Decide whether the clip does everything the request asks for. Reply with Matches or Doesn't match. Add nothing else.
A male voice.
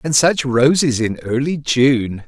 Matches